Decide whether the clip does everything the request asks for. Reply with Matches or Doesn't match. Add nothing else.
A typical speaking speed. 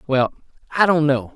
Matches